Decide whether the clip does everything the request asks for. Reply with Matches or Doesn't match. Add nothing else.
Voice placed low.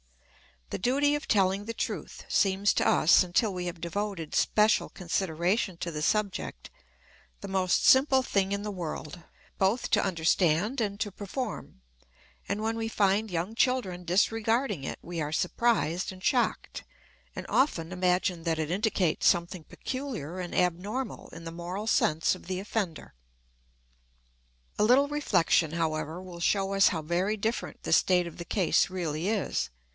Doesn't match